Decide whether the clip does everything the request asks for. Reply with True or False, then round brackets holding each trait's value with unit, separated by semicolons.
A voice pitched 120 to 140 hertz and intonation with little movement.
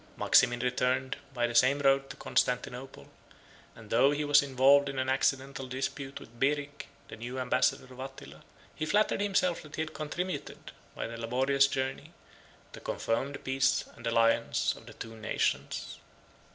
True (135 Hz; 2.1 semitones)